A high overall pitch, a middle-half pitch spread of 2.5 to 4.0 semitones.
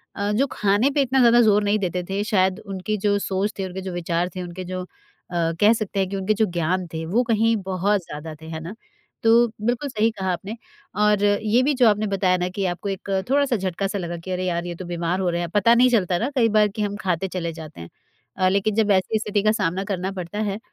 Yes: high, 195 Hz; average, 2.9 semitones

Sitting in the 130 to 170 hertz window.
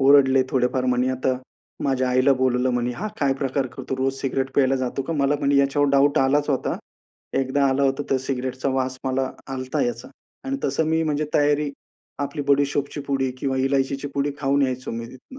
Yes: low, 135 Hz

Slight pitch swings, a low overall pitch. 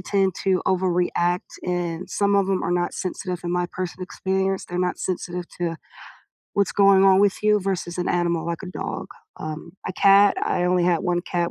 No: narrow, 1.6 semitones; medium, 180 Hz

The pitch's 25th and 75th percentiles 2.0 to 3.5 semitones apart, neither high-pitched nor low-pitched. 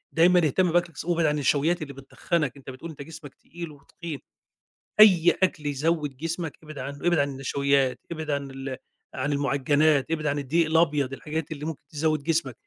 Yes: average, 2.8 semitones; medium, 150 Hz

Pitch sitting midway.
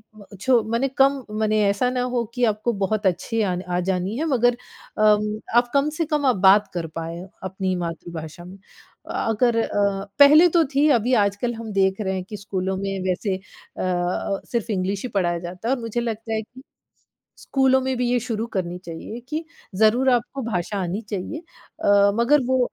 No: high, 215 Hz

